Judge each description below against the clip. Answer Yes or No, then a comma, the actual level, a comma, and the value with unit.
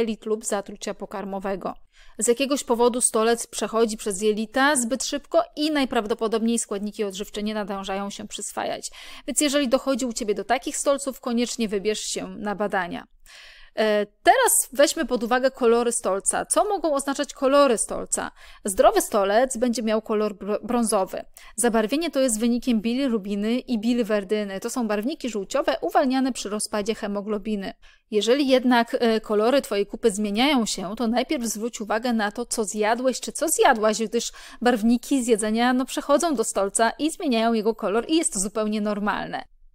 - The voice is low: No, high, 230 Hz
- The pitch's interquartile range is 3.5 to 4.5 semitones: Yes, average, 3.8 semitones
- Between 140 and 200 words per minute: Yes, average, 150 wpm